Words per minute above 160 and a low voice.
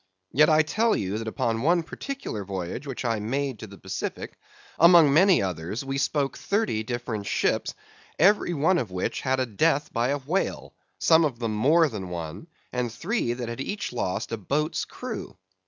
Yes: average, 190 wpm; low, 130 Hz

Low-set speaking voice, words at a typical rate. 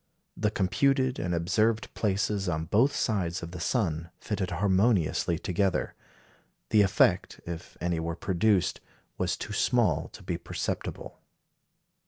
No: very low, 95 Hz; slow, 130 wpm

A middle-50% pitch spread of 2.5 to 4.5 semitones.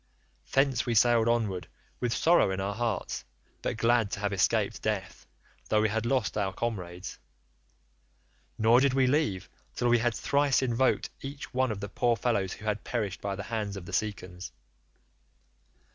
Yes: average, 3.5 semitones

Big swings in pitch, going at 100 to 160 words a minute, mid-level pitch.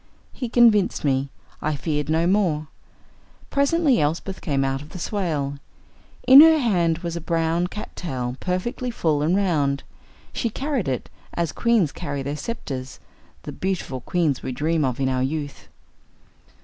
Yes: wide, 5.9 semitones; average, 150 wpm; medium, 165 Hz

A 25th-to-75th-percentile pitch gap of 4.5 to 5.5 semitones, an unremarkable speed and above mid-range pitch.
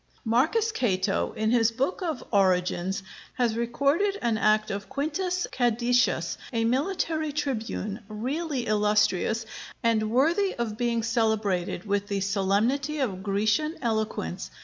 No: average, 4.9 semitones; slow, 125 wpm; high, 230 Hz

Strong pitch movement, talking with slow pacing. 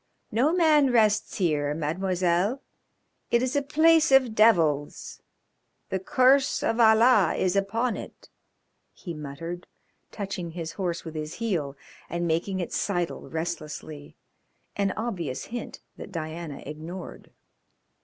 Yes: wide, 6.1 semitones; slow, 125 wpm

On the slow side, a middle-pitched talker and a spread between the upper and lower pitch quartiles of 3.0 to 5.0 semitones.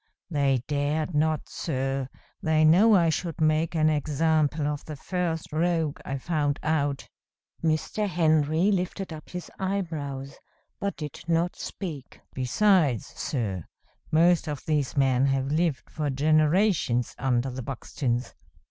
Yes: slow, 130 wpm; medium, 155 Hz; average, 3.3 semitones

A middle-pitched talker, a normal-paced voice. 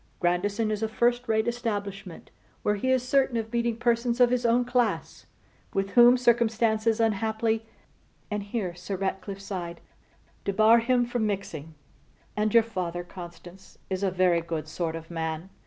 No: high, 215 Hz; average, 155 wpm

